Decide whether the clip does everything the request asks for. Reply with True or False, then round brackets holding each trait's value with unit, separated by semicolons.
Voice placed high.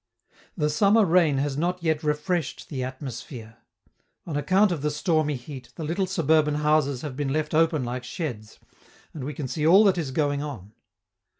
False (150 Hz)